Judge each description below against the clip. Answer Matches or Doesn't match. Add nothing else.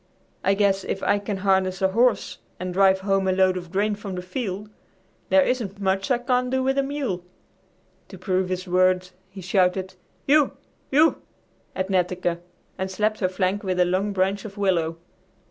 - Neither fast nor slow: Matches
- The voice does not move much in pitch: Matches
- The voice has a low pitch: Doesn't match